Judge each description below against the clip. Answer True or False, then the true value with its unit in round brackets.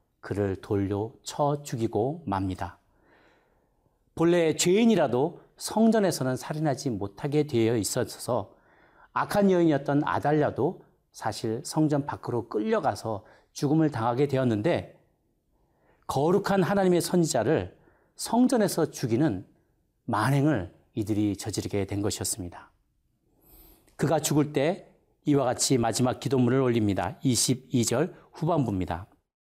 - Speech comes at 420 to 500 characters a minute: False (265 characters per minute)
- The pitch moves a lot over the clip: True (6.2 semitones)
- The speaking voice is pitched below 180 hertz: True (135 Hz)